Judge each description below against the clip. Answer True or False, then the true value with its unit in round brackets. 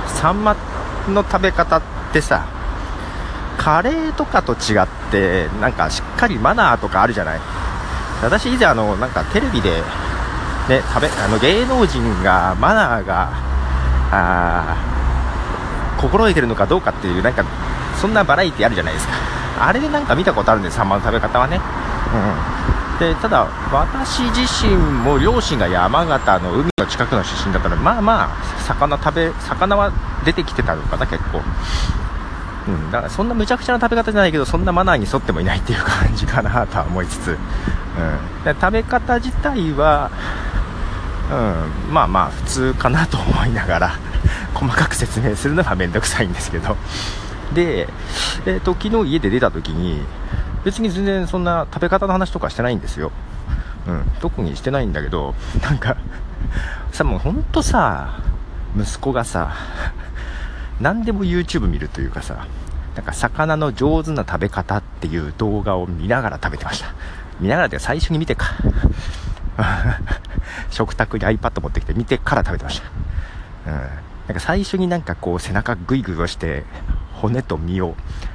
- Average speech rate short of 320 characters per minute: False (325 characters per minute)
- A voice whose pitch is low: True (95 Hz)